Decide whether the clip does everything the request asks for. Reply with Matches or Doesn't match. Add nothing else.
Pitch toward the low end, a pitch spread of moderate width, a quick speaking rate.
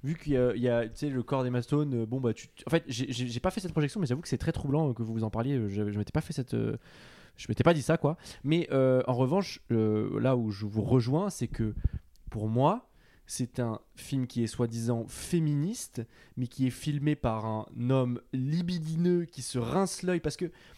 Matches